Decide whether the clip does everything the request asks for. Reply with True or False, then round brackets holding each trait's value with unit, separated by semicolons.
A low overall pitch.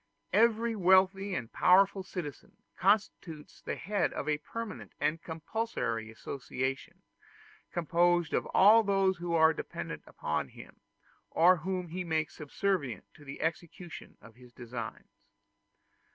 False (175 Hz)